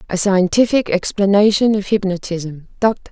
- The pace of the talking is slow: Yes, slow, 95 wpm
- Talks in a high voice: Yes, high, 200 Hz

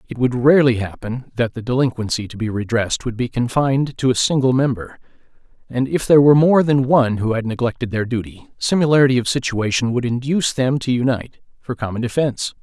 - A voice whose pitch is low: Yes, low, 125 Hz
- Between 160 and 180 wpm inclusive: No, average, 190 wpm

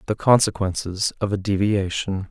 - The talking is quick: No, slow, 130 wpm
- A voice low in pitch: Yes, low, 100 Hz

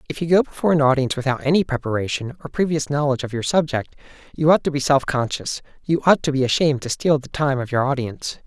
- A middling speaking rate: No, fast, 225 wpm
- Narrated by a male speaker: Yes, male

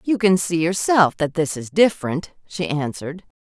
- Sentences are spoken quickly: No, average, 175 wpm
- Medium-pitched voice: Yes, medium, 170 Hz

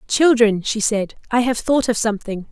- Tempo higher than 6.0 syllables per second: No, 5.1 syllables/s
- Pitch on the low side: No, high, 230 Hz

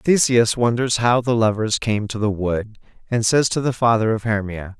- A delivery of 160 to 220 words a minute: Yes, average, 200 wpm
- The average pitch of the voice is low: Yes, low, 115 Hz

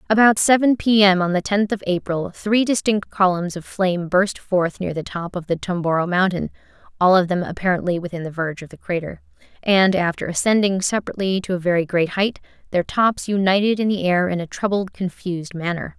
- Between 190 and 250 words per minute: Yes, average, 200 wpm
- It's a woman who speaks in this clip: Yes, female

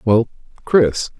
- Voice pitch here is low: Yes, low, 115 Hz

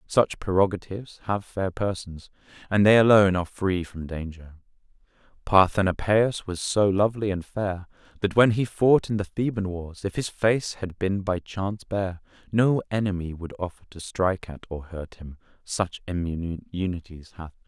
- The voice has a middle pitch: No, very low, 95 Hz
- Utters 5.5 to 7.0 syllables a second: No, 5.0 syllables/s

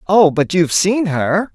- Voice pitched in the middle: Yes, medium, 180 Hz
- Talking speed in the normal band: Yes, average, 195 wpm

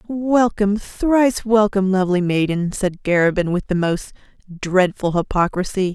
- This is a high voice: Yes, high, 195 Hz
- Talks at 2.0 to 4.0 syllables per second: No, 4.8 syllables/s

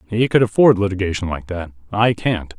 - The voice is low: Yes, low, 100 Hz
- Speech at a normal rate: Yes, average, 185 wpm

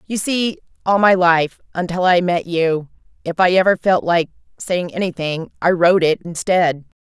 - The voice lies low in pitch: No, medium, 175 Hz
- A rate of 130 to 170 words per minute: Yes, average, 155 wpm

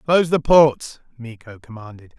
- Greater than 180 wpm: No, slow, 135 wpm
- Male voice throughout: Yes, male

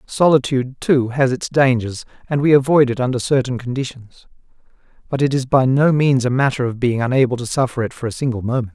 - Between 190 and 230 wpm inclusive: Yes, fast, 205 wpm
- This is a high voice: No, low, 130 Hz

